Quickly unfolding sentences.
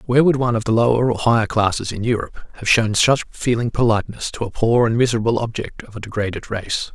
Yes: fast, 225 wpm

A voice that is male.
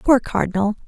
No: female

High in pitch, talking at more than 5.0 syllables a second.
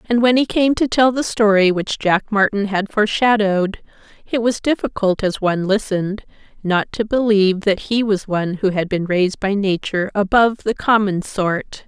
Yes: high, 205 Hz; 5.2 syllables/s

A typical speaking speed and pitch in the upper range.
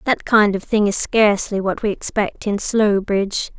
Yes: average, 185 wpm; high, 205 Hz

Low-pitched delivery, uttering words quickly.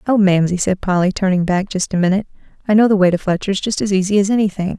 No: high, 195 Hz; fast, 250 wpm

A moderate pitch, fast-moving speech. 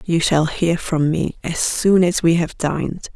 Yes: medium, 165 Hz; fast, 210 wpm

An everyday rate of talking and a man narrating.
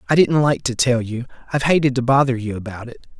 No: fast, 225 wpm; male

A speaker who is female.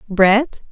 Yes: female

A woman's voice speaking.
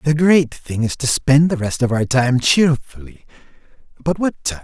No: male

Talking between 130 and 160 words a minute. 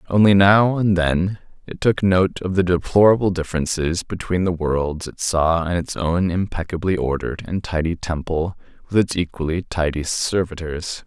Yes: average, 155 wpm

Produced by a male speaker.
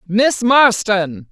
No: female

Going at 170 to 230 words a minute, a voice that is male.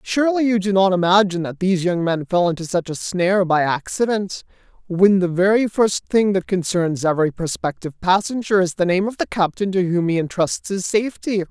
Yes: average, 200 wpm; male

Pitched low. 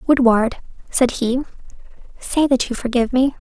No: very high, 250 Hz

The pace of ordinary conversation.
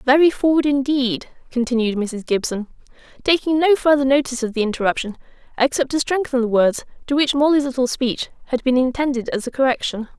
Yes: average, 170 wpm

